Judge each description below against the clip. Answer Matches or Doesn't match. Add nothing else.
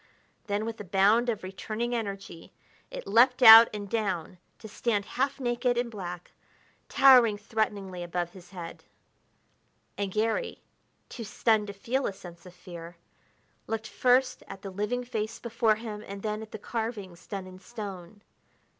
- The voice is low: Doesn't match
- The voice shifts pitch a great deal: Doesn't match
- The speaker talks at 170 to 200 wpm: Doesn't match